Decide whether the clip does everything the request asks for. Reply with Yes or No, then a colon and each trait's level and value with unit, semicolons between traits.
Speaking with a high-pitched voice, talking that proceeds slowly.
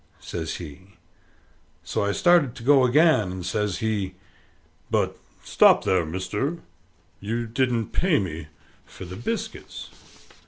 No: low, 105 Hz; slow, 125 wpm